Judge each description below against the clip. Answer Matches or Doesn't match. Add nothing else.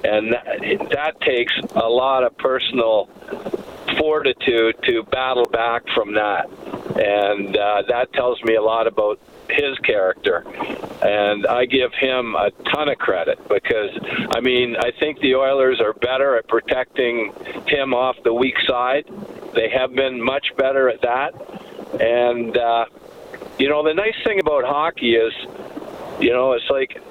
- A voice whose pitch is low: Matches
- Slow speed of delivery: Doesn't match